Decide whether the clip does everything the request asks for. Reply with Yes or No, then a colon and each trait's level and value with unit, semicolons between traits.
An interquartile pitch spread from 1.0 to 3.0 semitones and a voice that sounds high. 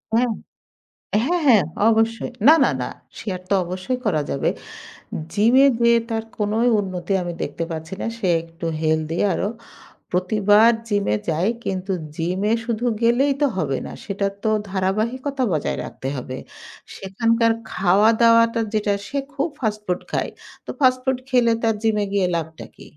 No: average, 4.2 semitones; high, 210 Hz